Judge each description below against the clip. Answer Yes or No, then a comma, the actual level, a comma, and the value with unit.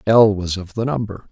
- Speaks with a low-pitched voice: Yes, low, 105 Hz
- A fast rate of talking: No, average, 180 wpm